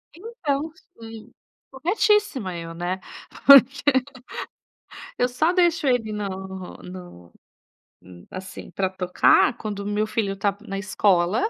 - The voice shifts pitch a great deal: Yes, wide, 6.9 semitones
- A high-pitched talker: Yes, high, 215 Hz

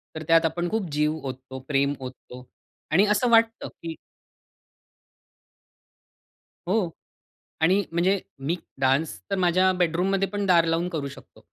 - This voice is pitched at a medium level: Yes, medium, 170 Hz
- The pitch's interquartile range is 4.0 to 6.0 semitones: Yes, average, 4.3 semitones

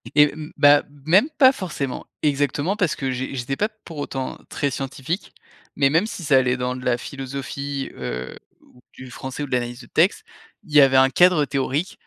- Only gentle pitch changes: No, average, 3.1 semitones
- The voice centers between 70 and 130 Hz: No, medium, 140 Hz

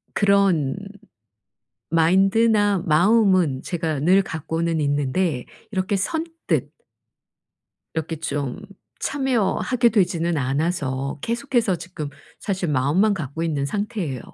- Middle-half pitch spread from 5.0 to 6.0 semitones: Yes, wide, 5.4 semitones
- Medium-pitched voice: Yes, medium, 175 Hz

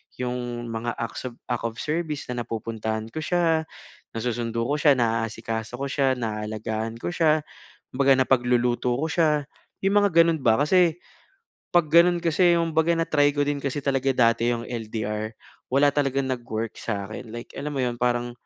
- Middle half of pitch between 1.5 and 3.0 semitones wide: No, average, 4.6 semitones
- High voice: No, low, 125 Hz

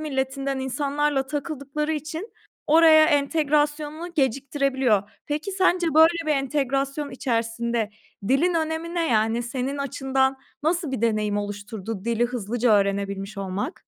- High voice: Yes, very high, 275 Hz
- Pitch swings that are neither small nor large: Yes, average, 4.7 semitones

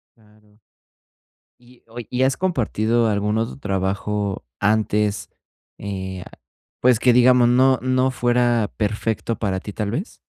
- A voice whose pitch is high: No, low, 110 Hz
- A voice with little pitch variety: No, average, 3.0 semitones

